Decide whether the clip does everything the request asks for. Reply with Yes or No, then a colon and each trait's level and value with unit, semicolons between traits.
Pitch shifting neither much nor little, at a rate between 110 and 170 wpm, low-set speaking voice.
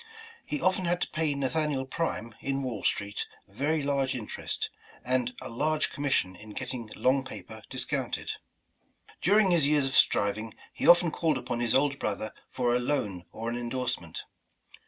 Yes: average, 4.3 semitones; average, 160 wpm; low, 130 Hz